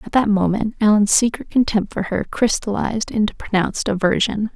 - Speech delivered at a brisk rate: No, average, 160 wpm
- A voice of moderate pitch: No, high, 210 Hz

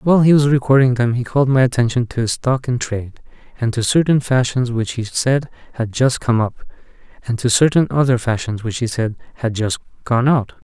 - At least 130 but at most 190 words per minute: No, fast, 205 wpm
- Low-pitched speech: Yes, low, 125 Hz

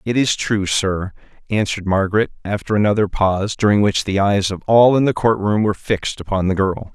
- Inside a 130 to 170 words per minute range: No, average, 200 wpm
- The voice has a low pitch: Yes, low, 100 Hz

